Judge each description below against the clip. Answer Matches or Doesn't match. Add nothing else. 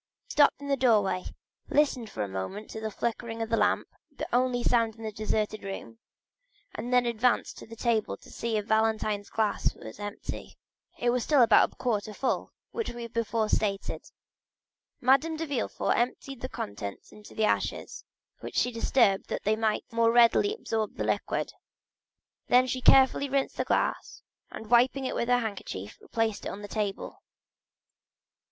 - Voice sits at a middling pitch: Doesn't match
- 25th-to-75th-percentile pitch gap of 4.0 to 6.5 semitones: Doesn't match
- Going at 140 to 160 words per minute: Doesn't match